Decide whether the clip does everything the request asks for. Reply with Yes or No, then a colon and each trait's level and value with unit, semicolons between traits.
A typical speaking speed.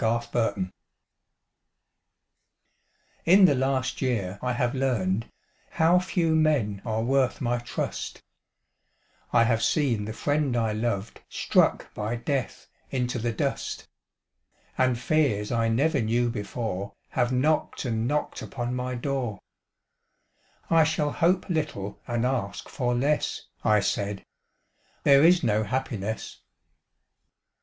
No: slow, 120 wpm